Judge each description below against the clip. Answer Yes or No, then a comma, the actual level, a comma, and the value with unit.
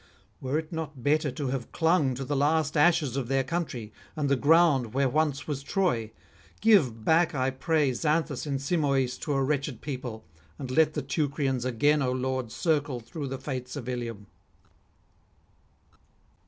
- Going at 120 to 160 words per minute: No, average, 170 wpm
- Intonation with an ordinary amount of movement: Yes, average, 3.2 semitones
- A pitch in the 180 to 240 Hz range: No, medium, 140 Hz